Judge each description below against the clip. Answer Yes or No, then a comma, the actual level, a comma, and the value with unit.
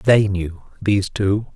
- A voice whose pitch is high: No, low, 100 Hz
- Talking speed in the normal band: Yes, average, 155 wpm